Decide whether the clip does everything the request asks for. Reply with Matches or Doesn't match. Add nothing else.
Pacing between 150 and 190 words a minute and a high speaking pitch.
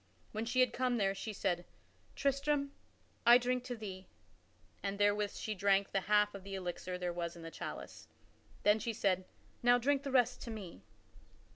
Matches